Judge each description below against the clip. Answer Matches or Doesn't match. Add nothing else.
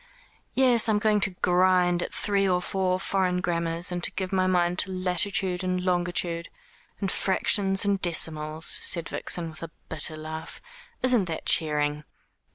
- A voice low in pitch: Doesn't match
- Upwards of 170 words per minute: Doesn't match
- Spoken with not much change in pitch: Matches